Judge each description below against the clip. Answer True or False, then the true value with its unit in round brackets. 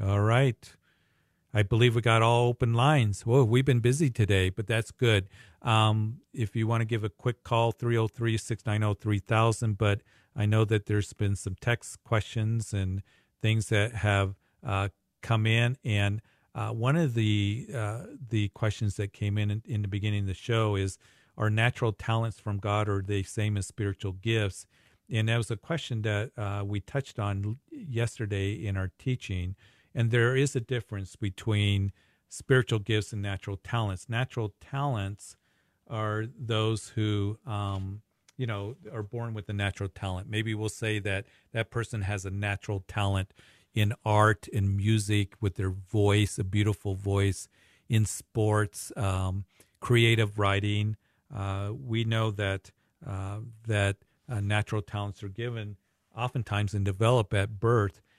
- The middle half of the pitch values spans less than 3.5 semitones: True (2.4 semitones)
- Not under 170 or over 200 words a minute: False (155 wpm)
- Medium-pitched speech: False (105 Hz)